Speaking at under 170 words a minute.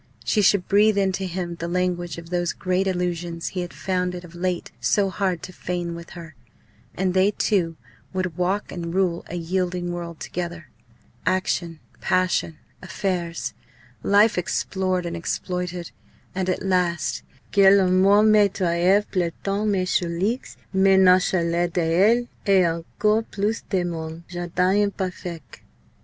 Yes: average, 145 wpm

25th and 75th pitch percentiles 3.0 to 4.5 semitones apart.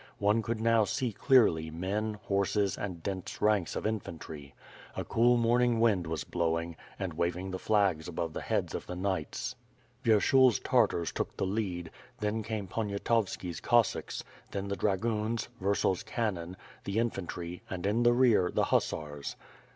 Yes: average, 4.2 semitones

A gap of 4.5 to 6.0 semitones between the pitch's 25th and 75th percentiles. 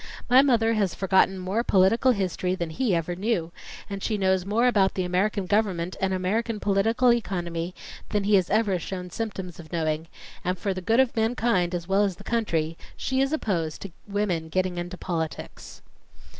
No: average, 3.8 semitones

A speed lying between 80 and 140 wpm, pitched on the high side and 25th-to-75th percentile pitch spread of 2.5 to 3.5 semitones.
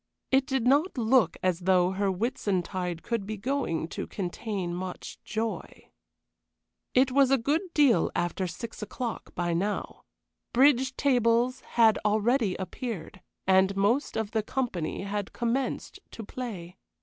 No: slow, 135 wpm; high, 220 Hz; average, 5.2 semitones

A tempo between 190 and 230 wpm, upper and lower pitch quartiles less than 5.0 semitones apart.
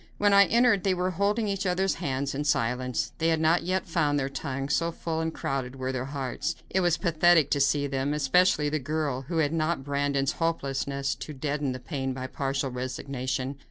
Yes: average, 200 wpm; average, 3.8 semitones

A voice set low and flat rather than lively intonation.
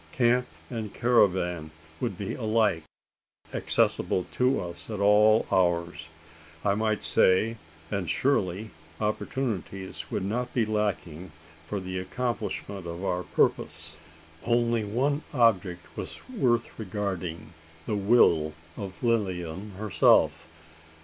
No: low, 100 Hz; average, 4.3 semitones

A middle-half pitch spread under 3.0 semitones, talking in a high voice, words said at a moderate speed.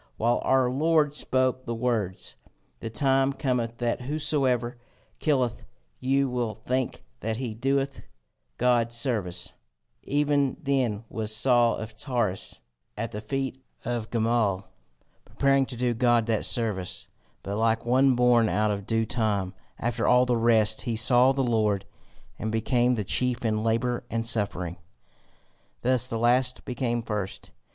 No: narrow, 2.6 semitones; low, 120 Hz; average, 145 wpm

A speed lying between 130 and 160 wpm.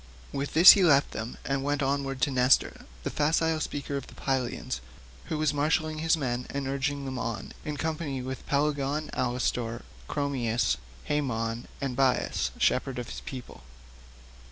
Yes: average, 155 wpm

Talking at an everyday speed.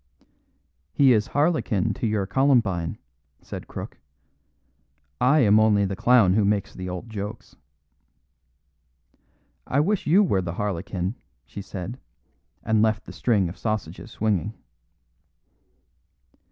No: slow, 120 wpm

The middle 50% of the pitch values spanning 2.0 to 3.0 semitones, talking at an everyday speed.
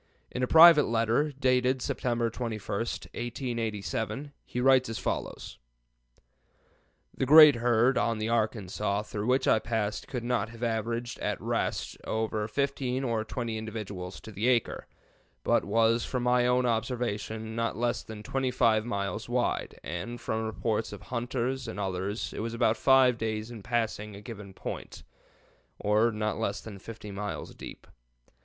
Yes: narrow, 2.5 semitones; average, 150 wpm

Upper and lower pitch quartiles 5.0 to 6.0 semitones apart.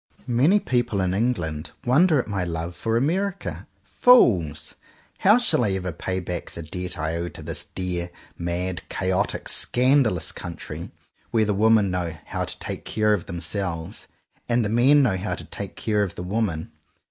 Yes: wide, 5.6 semitones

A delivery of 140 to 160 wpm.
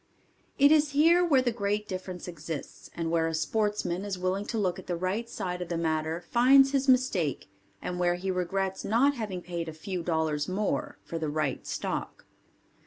No: average, 190 wpm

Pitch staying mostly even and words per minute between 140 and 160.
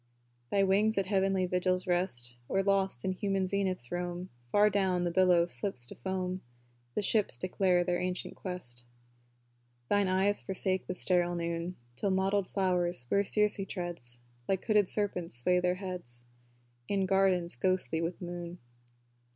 Yes: narrow, 1.8 semitones; average, 150 wpm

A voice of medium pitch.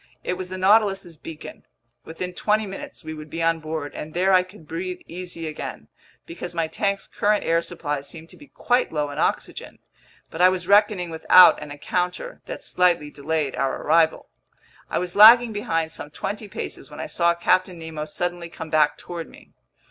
Yes: medium, 170 Hz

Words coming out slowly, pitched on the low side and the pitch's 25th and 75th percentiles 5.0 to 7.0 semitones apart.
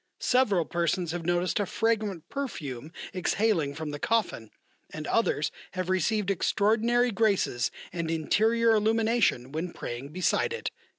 No: slow, 130 wpm; medium, 185 Hz; wide, 5.6 semitones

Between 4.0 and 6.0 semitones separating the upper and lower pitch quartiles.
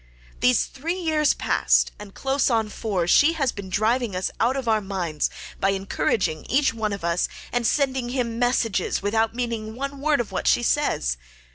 Yes: average, 5.0 semitones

